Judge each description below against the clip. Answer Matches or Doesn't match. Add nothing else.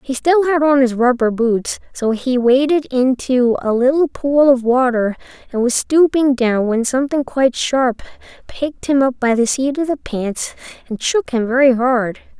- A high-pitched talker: Matches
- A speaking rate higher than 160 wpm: Matches